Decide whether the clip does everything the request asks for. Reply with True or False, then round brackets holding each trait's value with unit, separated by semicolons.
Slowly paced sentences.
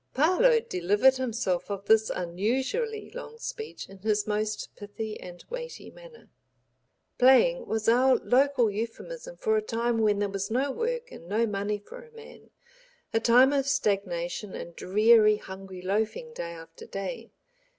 False (150 wpm)